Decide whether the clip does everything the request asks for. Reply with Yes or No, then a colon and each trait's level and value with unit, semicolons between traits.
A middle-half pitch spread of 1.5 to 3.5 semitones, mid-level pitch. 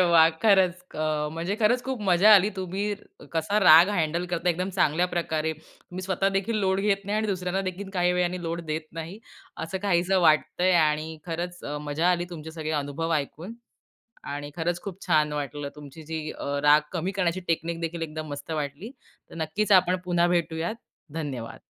Yes: average, 3.0 semitones; medium, 170 Hz